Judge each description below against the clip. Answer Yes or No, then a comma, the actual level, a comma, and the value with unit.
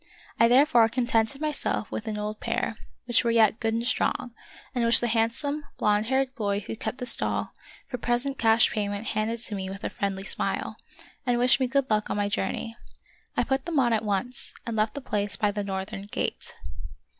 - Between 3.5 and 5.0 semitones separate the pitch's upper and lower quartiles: No, average, 2.9 semitones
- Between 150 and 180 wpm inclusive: No, fast, 205 wpm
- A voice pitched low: No, high, 230 Hz